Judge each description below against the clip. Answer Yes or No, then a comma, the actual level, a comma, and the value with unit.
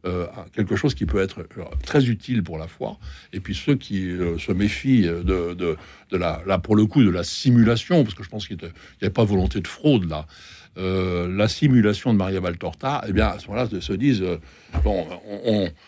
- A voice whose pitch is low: Yes, very low, 95 Hz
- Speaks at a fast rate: Yes, fast, 225 wpm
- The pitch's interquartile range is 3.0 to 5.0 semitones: Yes, average, 3.8 semitones